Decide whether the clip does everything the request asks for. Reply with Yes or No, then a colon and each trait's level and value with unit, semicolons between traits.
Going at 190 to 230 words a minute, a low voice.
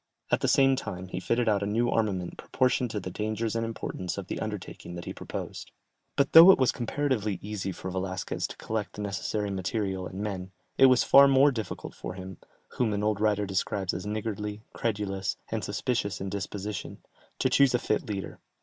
Yes: average, 195 wpm; low, 105 Hz